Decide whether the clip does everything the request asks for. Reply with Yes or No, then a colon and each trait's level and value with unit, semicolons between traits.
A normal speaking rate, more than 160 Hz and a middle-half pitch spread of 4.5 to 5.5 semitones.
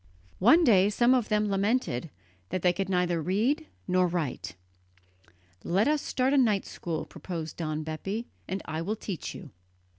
Yes: average, 160 wpm; high, 190 Hz; average, 4.8 semitones